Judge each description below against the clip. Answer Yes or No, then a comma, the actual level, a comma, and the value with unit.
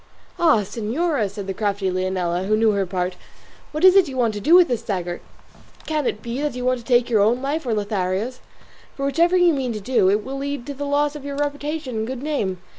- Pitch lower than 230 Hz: No, high, 245 Hz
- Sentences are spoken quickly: Yes, fast, 240 wpm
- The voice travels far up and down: Yes, wide, 6.0 semitones